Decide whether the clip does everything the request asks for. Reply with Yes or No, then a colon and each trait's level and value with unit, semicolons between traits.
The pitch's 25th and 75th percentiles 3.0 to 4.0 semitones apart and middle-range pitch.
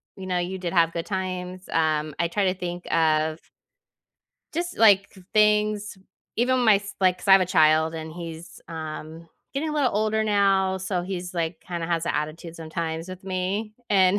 Yes: average, 3.4 semitones; medium, 180 Hz